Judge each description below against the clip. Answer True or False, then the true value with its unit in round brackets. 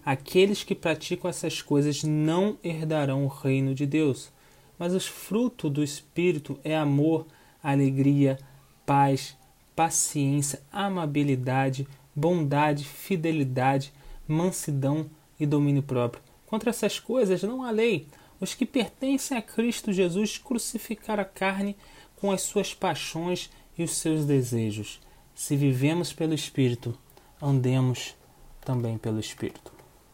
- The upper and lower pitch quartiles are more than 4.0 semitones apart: True (5.2 semitones)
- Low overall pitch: False (155 Hz)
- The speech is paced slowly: True (115 wpm)